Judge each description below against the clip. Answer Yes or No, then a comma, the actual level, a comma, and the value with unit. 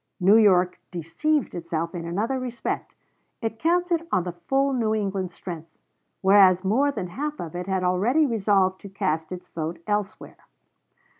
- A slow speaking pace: No, average, 155 wpm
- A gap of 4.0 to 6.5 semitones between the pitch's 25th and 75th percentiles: Yes, average, 5.3 semitones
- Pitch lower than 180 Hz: No, high, 195 Hz